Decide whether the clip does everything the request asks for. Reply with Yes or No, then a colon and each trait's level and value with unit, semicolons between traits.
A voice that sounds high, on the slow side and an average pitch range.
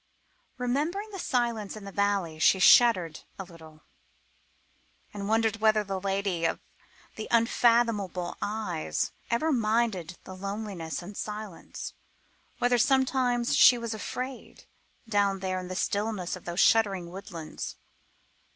Yes: high, 205 Hz; slow, 125 wpm; average, 4.1 semitones